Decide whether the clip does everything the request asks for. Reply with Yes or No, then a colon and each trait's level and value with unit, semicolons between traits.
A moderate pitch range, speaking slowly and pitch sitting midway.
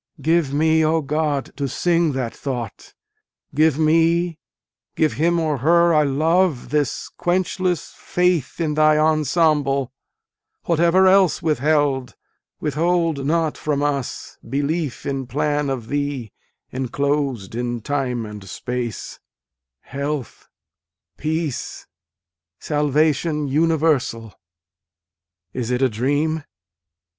Yes: average, 3.1 semitones; slow, 105 wpm; medium, 150 Hz